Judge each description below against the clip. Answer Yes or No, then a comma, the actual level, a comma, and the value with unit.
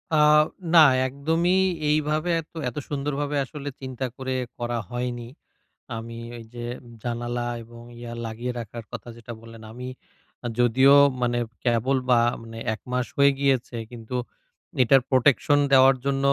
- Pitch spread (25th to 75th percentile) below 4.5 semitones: Yes, average, 2.7 semitones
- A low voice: Yes, low, 125 Hz